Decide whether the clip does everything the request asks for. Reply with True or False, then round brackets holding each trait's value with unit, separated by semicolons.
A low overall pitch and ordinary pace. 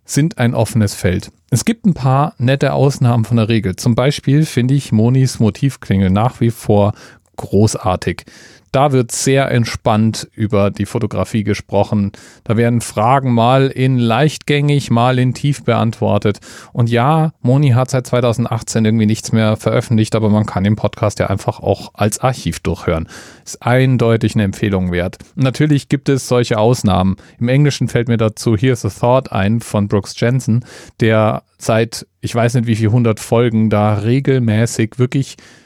True (115 Hz; 160 wpm)